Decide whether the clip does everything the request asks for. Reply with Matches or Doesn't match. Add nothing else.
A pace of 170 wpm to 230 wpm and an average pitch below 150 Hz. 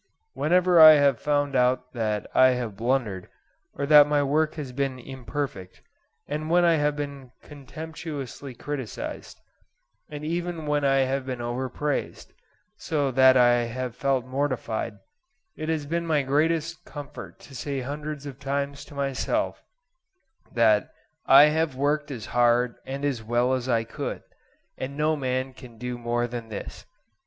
Doesn't match